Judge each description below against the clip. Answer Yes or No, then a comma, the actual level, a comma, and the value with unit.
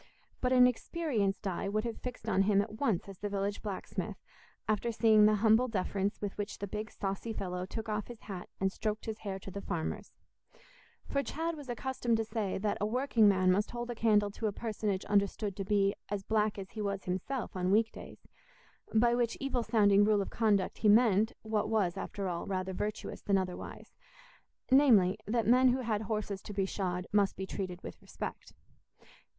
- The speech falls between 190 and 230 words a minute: Yes, average, 195 wpm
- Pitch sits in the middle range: No, high, 210 Hz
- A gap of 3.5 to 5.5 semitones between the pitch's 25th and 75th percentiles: No, narrow, 2.6 semitones